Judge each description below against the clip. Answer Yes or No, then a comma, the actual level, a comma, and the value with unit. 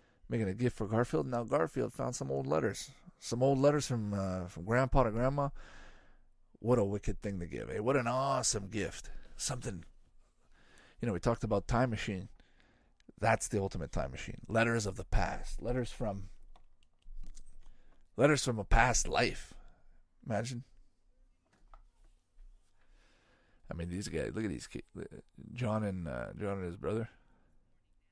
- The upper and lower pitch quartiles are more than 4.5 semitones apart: Yes, average, 5.0 semitones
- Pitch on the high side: No, low, 105 Hz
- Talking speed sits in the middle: Yes, average, 155 wpm